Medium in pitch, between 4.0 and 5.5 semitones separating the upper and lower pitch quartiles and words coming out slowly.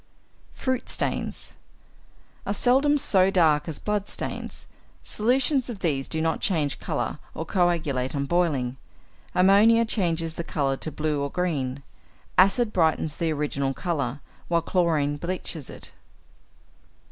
Yes: medium, 165 Hz; average, 5.1 semitones; slow, 130 wpm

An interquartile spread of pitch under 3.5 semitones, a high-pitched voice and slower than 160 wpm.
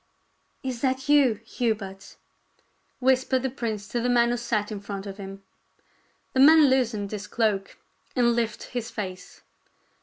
No: average, 4.0 semitones; high, 235 Hz; average, 150 wpm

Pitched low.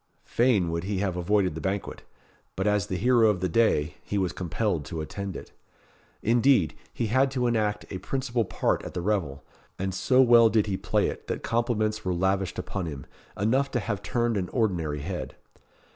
Yes: low, 100 Hz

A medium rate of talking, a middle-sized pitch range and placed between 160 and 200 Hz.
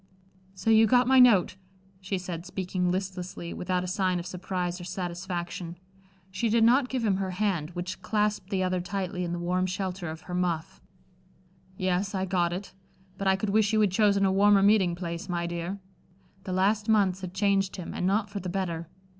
No: average, 195 wpm; narrow, 2.1 semitones; medium, 185 Hz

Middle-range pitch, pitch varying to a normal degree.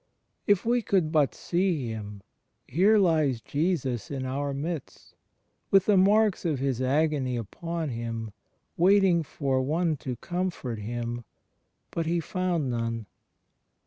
No: medium, 150 Hz; wide, 6.1 semitones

